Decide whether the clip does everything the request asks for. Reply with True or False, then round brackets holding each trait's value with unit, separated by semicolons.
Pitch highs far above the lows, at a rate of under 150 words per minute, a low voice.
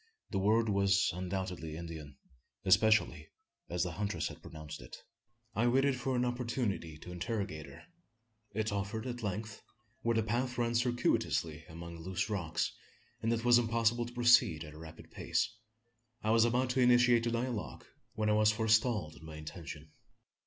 False (5.8 semitones; 160 wpm; 105 Hz)